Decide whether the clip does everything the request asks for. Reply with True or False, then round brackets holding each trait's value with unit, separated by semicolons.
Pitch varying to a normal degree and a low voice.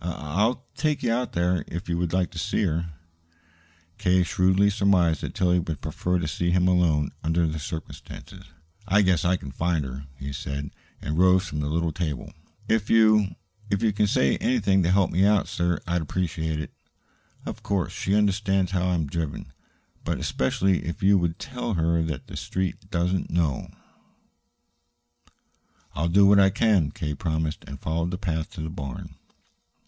True (3.3 semitones; 90 Hz)